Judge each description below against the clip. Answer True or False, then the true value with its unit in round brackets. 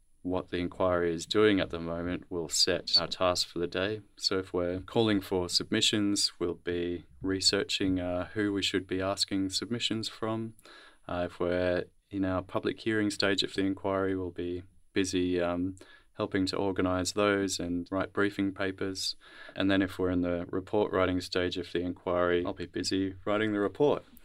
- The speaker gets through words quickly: False (180 wpm)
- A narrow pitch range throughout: True (2.0 semitones)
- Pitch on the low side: True (95 Hz)